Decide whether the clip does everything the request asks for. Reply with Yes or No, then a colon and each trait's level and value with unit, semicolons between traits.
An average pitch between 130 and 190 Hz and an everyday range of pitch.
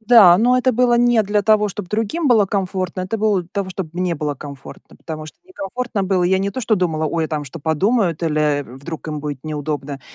No: medium, 185 Hz; wide, 5.7 semitones